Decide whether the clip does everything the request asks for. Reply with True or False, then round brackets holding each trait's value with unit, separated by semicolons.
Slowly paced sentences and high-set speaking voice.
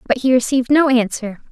False (200 wpm; 250 Hz)